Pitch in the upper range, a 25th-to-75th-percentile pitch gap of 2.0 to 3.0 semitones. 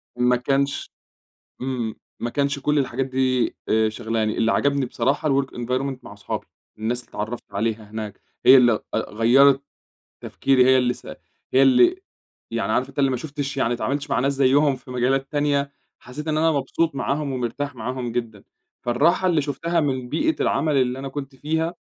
No: low, 135 Hz; average, 2.7 semitones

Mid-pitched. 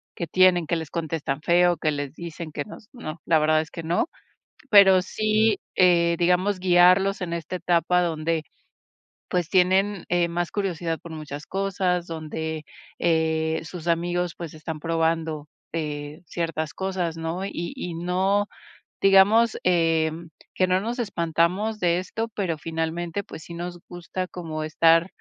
Yes: medium, 170 Hz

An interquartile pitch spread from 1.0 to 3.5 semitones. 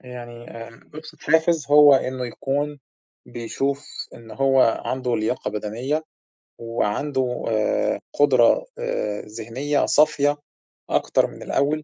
No: average, 3.9 semitones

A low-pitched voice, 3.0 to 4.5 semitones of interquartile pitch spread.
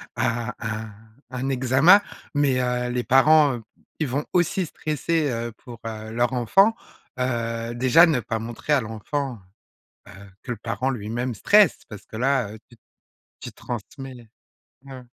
Yes: low, 125 Hz; average, 3.3 semitones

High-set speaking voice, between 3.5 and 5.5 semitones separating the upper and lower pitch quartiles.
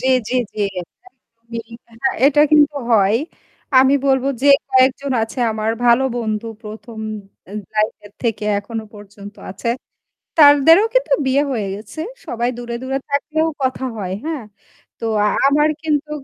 Yes: high, 245 Hz; average, 4.8 semitones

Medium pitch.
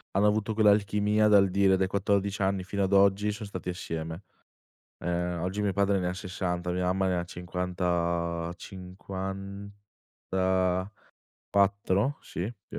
No: very low, 95 Hz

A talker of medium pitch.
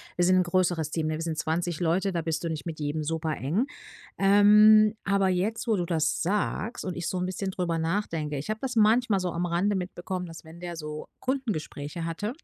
Yes: medium, 175 Hz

